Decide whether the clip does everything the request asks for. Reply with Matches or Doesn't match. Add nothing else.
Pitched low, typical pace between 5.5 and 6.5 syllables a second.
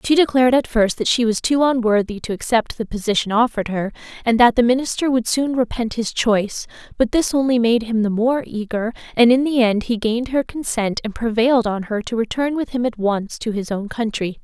Doesn't match